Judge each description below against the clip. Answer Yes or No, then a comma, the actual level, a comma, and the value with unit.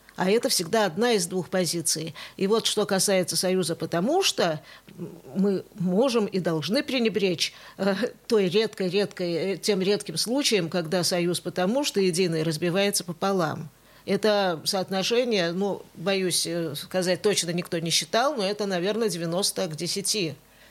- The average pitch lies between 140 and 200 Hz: Yes, medium, 185 Hz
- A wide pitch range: No, average, 2.9 semitones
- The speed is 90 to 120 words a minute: No, average, 135 wpm